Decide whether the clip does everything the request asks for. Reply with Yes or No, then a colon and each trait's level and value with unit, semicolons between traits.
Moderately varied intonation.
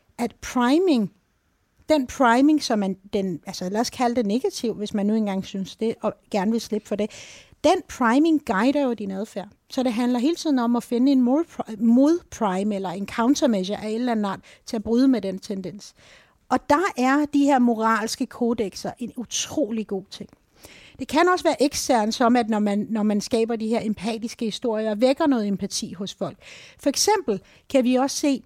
Yes: average, 4.1 semitones